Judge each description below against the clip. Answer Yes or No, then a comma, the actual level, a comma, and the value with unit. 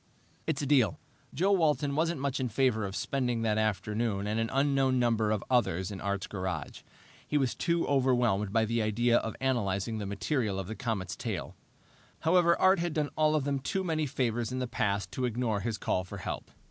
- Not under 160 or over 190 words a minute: No, average, 200 wpm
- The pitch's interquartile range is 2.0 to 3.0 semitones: No, average, 5.0 semitones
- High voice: No, low, 120 Hz